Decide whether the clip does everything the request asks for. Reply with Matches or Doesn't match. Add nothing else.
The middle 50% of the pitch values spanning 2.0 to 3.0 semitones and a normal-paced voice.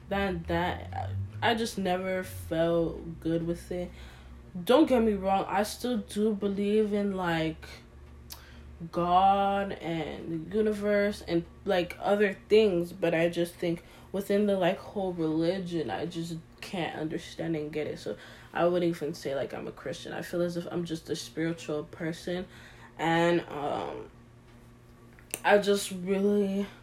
Doesn't match